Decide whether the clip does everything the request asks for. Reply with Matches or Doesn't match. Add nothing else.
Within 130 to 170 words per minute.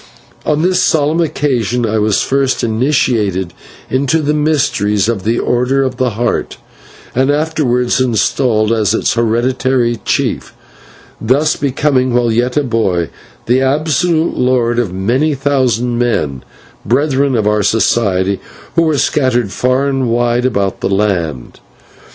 Matches